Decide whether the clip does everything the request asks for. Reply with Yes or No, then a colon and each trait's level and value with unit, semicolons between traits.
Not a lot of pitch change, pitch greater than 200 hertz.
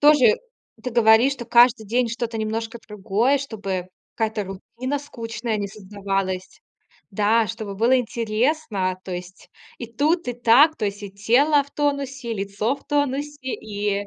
No: average, 4.1 semitones; high, 230 Hz